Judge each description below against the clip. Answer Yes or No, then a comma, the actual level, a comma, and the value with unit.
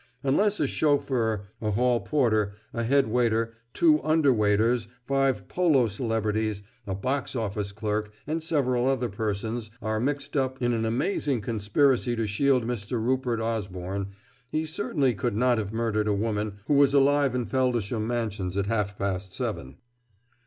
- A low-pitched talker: Yes, low, 115 Hz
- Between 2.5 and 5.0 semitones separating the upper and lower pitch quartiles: Yes, average, 4.0 semitones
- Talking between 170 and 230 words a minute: No, average, 155 wpm